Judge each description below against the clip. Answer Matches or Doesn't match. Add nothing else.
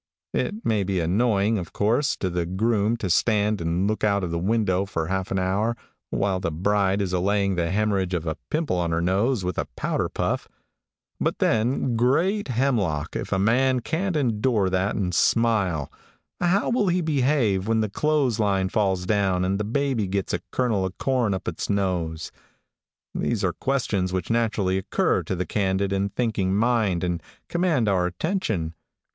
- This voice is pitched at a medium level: Doesn't match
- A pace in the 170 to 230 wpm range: Matches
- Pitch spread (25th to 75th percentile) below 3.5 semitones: Doesn't match